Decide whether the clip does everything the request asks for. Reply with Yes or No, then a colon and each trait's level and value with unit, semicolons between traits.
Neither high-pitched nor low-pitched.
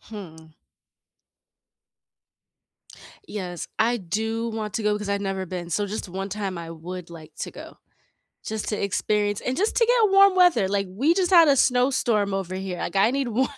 No: high, 210 Hz